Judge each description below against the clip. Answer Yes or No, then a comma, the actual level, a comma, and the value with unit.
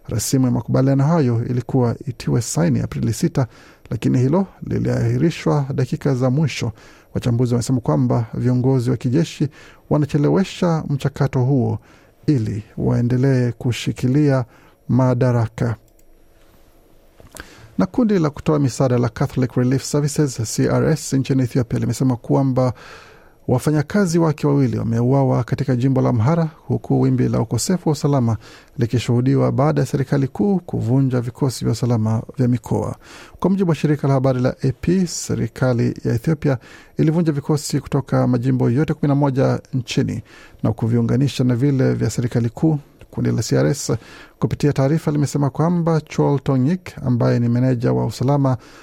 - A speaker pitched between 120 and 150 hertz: Yes, low, 135 Hz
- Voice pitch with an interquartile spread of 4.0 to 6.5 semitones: No, average, 3.2 semitones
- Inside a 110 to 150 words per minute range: Yes, average, 130 wpm